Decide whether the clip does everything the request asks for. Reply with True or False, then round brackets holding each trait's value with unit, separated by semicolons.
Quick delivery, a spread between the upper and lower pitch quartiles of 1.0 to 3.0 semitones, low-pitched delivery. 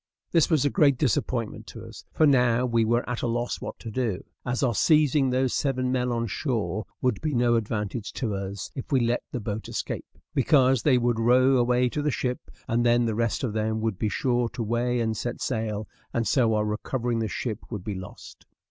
True (220 wpm; 2.5 semitones; 120 Hz)